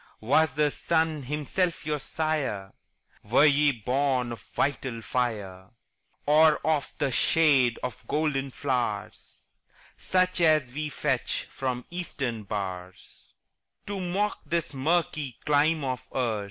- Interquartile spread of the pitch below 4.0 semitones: No, average, 4.3 semitones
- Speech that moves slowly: Yes, slow, 120 wpm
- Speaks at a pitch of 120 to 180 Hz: Yes, medium, 140 Hz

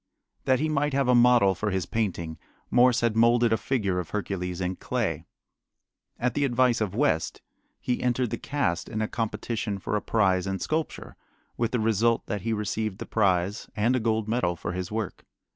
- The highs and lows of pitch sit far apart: No, average, 3.9 semitones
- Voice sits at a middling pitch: No, low, 110 Hz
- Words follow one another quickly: No, average, 195 wpm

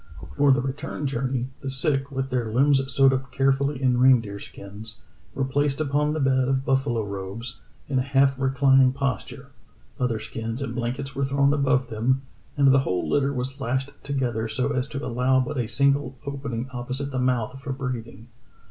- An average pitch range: No, narrow, 1.8 semitones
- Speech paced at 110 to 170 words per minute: No, average, 180 wpm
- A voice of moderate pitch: No, low, 130 Hz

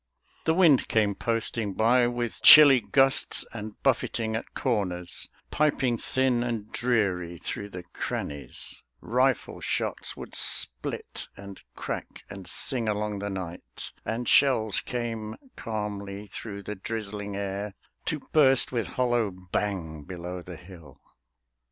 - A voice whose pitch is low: Yes, low, 105 Hz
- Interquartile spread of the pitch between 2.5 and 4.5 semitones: Yes, average, 3.8 semitones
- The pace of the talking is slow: Yes, slow, 125 wpm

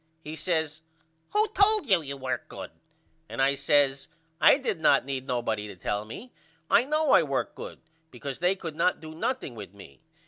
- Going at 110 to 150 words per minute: No, average, 185 wpm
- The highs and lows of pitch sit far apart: Yes, wide, 6.5 semitones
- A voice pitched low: No, medium, 150 Hz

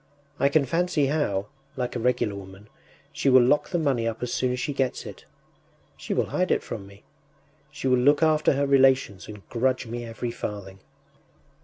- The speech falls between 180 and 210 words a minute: Yes, average, 190 wpm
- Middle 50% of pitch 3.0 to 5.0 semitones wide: Yes, average, 3.9 semitones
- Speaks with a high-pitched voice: No, low, 125 Hz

